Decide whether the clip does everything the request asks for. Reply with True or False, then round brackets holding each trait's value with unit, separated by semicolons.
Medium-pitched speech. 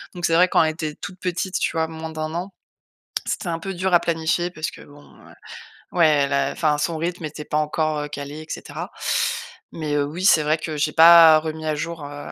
True (160 Hz)